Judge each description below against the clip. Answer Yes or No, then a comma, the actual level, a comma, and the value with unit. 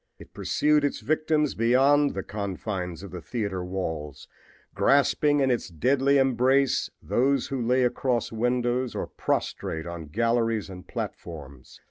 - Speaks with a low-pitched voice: Yes, low, 120 Hz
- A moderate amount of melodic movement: No, wide, 6.3 semitones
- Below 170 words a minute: Yes, slow, 135 wpm